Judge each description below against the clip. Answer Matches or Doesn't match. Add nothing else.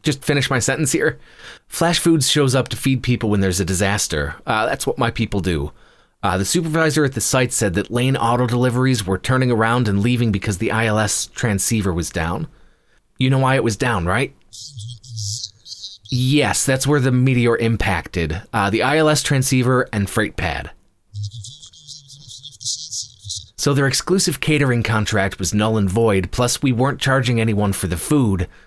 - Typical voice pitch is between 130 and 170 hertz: Doesn't match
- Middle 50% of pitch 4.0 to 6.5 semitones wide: Matches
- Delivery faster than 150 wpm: Matches